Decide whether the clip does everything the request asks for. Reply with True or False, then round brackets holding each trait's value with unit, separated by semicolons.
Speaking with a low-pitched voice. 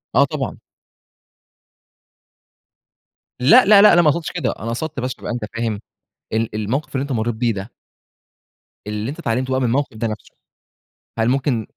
True (125 Hz)